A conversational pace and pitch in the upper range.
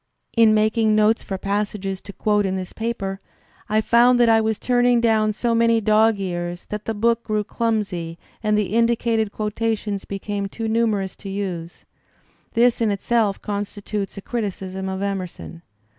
Yes: average, 160 wpm; high, 210 Hz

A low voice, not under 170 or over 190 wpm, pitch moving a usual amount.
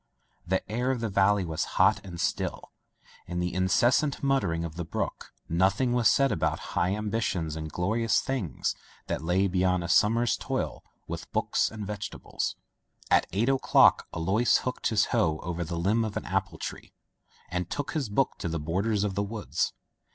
Yes: low, 100 Hz; average, 180 wpm; average, 4.7 semitones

